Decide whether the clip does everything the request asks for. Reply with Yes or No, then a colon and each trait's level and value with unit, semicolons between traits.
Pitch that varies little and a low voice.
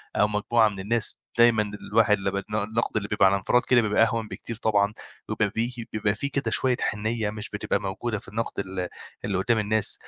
Yes: narrow, 2.0 semitones; low, 110 Hz